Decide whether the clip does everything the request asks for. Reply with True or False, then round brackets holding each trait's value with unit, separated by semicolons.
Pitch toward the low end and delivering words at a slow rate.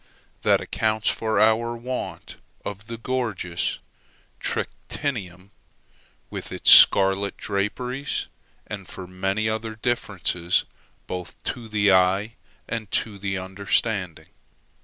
True (105 Hz; 105 wpm)